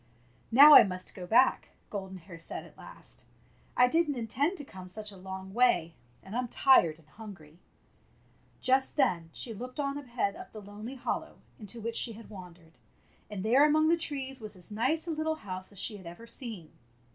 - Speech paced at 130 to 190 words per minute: No, average, 200 wpm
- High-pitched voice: Yes, high, 220 Hz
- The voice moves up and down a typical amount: No, wide, 5.9 semitones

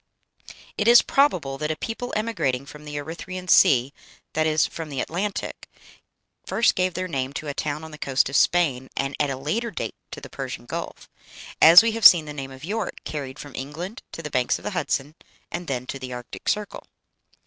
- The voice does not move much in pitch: No, average, 5.2 semitones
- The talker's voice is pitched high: No, medium, 150 Hz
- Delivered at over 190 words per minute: Yes, fast, 205 wpm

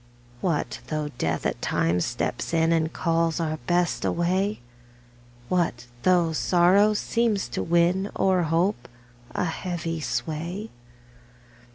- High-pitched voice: No, medium, 170 Hz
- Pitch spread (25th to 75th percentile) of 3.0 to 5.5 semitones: No, narrow, 2.5 semitones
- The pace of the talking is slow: Yes, slow, 120 wpm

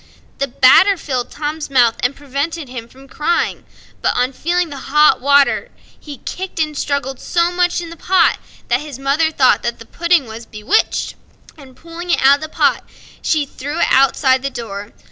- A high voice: Yes, very high, 280 Hz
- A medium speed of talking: Yes, average, 185 wpm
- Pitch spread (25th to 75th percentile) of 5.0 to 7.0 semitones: No, average, 4.1 semitones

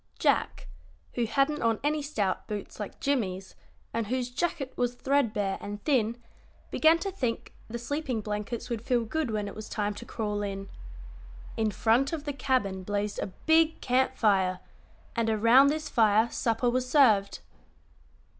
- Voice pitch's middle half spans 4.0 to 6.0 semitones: Yes, average, 4.7 semitones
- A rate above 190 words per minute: No, average, 160 wpm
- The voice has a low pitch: No, high, 230 Hz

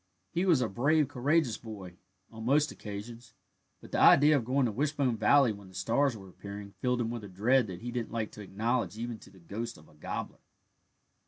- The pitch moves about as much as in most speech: Yes, average, 4.5 semitones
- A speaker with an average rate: No, fast, 215 wpm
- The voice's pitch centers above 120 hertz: No, low, 115 Hz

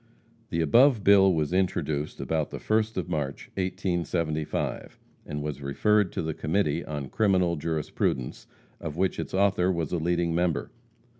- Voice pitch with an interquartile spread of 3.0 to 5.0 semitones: Yes, average, 3.6 semitones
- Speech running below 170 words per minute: Yes, average, 150 wpm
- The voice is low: Yes, very low, 85 Hz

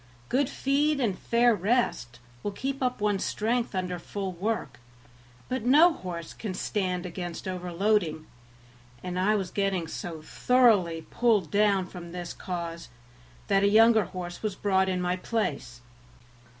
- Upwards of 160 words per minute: No, average, 145 wpm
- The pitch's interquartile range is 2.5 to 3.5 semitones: No, average, 4.2 semitones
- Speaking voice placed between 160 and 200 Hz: Yes, high, 190 Hz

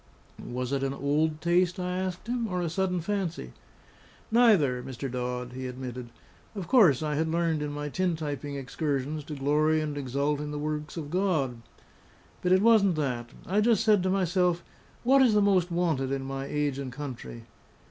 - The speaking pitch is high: No, medium, 155 Hz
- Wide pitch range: No, average, 4.9 semitones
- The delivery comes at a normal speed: Yes, average, 180 wpm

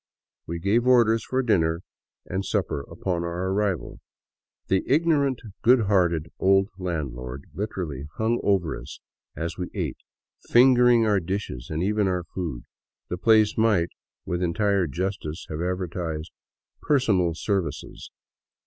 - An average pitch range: Yes, average, 4.4 semitones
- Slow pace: Yes, slow, 130 wpm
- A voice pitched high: No, very low, 95 Hz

